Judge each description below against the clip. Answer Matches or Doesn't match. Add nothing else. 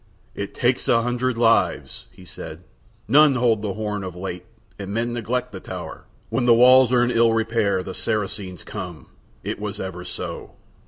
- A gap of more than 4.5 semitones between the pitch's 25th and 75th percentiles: Doesn't match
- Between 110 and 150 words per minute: Doesn't match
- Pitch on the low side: Matches